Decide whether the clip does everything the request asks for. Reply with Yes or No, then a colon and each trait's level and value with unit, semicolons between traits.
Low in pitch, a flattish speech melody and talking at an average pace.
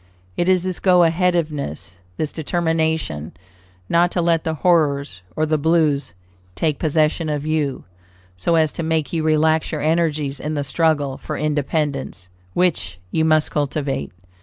No: medium, 155 Hz; narrow, 2.2 semitones; average, 150 wpm